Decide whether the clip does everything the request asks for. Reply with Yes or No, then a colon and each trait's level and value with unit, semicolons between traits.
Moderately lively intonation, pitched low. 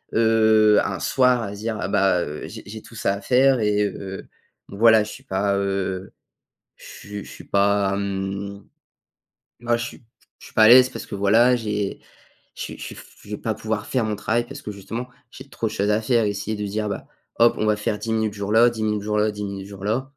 No: narrow, 2.1 semitones; low, 105 Hz